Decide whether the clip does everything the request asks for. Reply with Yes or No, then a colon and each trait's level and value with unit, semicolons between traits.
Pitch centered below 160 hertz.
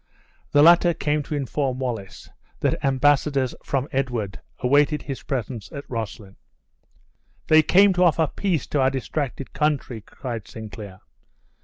Yes: low, 135 Hz